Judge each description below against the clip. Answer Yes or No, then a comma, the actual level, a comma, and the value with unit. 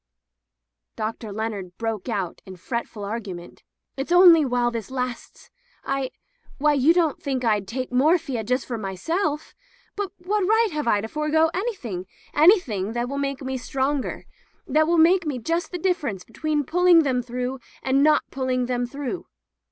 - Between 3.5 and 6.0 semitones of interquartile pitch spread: Yes, wide, 5.6 semitones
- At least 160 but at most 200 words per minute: Yes, average, 175 wpm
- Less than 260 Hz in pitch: No, very high, 265 Hz